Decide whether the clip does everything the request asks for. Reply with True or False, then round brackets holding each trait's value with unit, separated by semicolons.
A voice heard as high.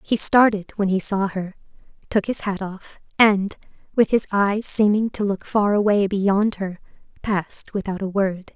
True (200 Hz)